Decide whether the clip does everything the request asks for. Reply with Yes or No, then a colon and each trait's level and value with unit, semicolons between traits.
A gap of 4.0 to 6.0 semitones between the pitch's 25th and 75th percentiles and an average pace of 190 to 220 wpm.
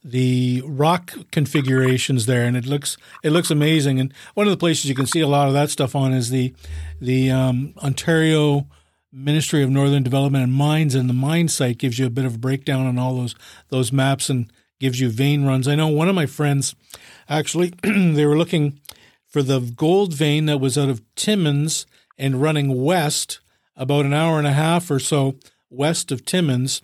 No: average, 2.9 semitones; average, 200 wpm